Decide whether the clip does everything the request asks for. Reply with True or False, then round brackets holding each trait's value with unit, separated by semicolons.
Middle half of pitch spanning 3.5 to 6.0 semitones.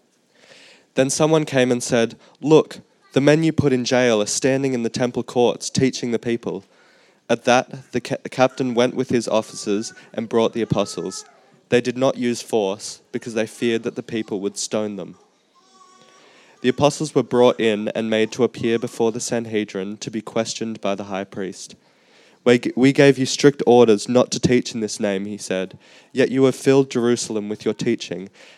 False (3.0 semitones)